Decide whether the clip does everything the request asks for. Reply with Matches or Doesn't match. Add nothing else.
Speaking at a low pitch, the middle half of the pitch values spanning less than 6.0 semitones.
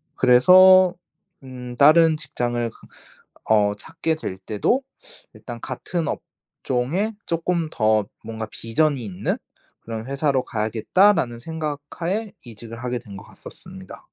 Doesn't match